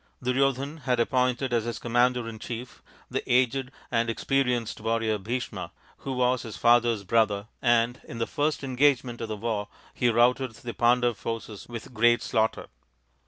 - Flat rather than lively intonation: Yes, narrow, 1.7 semitones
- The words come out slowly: No, average, 165 wpm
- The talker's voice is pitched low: Yes, low, 120 Hz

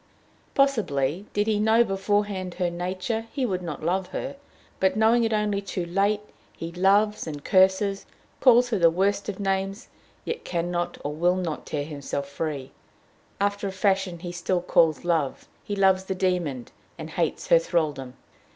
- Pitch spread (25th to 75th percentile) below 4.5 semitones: Yes, average, 3.4 semitones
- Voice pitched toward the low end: No, medium, 185 Hz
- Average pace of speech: Yes, average, 170 wpm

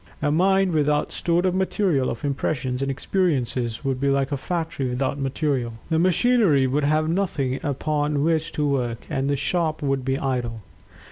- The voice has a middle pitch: Yes, medium, 145 Hz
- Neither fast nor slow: Yes, average, 175 wpm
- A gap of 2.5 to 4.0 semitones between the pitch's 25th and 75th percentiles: Yes, average, 3.5 semitones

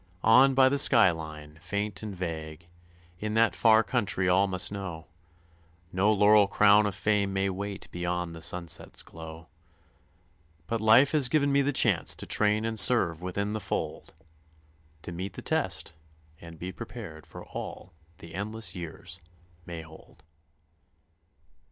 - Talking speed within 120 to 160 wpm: Yes, average, 150 wpm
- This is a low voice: Yes, low, 100 Hz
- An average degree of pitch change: Yes, average, 4.3 semitones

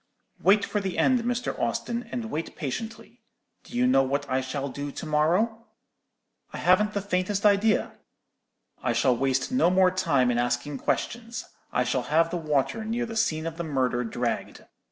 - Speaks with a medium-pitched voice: Yes, medium, 170 Hz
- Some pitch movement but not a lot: No, wide, 8.3 semitones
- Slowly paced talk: No, average, 175 wpm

